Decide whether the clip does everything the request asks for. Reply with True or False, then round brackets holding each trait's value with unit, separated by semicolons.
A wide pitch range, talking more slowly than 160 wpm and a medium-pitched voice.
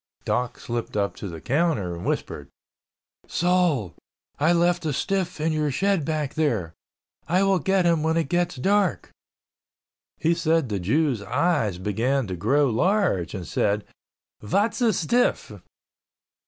True (8.5 semitones; 145 wpm; 155 Hz)